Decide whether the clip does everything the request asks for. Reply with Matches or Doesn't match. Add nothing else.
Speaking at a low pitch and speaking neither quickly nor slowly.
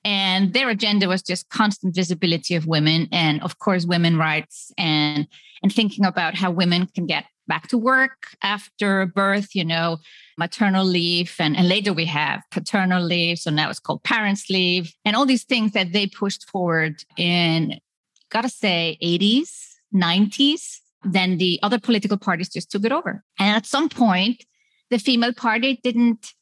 Doesn't match